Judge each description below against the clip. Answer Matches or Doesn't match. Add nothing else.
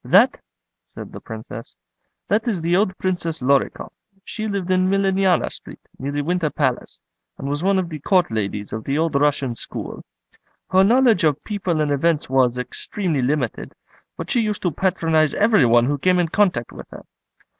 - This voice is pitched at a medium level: Matches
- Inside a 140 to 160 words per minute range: Doesn't match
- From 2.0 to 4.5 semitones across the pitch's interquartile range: Doesn't match